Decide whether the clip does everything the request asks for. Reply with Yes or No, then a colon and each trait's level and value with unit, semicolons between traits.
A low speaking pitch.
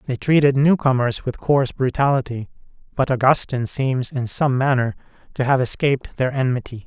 Yes: low, 130 Hz